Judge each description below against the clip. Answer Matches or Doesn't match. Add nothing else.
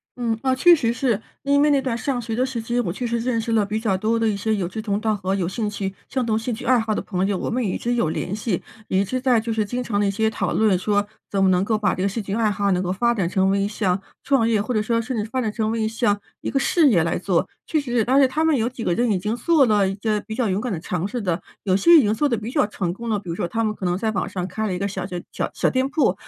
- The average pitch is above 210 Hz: Matches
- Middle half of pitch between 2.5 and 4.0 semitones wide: Matches